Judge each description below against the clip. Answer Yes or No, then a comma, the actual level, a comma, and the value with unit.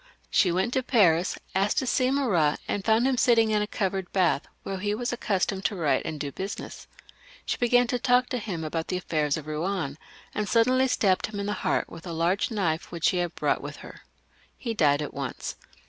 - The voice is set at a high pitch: Yes, high, 195 Hz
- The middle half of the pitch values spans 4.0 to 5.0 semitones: No, wide, 5.5 semitones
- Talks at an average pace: No, fast, 215 wpm